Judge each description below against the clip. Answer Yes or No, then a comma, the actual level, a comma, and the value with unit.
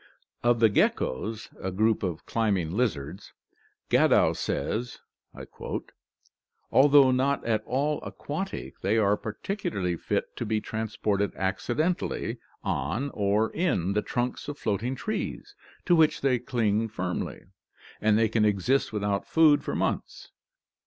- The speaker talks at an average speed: No, slow, 130 wpm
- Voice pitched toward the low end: Yes, low, 110 Hz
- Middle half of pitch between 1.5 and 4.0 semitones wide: No, average, 4.6 semitones